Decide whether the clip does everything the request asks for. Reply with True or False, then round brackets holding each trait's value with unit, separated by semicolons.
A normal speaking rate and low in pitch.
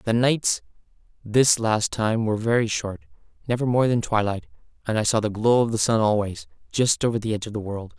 False (210 wpm; 110 Hz)